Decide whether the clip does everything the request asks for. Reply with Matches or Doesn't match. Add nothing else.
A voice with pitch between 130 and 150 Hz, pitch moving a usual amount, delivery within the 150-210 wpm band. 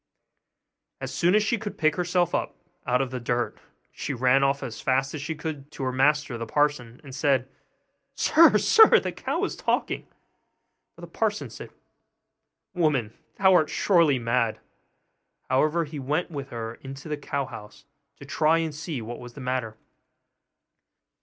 Matches